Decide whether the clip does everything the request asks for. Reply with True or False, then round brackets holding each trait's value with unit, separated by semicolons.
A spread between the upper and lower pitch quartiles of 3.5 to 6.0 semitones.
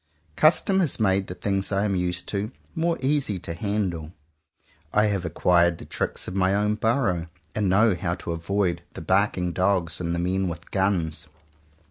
False (3.1 semitones)